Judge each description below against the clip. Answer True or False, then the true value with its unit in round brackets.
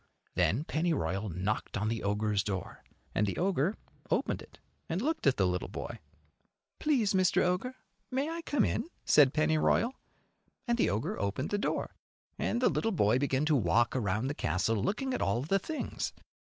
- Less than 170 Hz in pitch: True (140 Hz)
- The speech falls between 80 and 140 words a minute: False (175 wpm)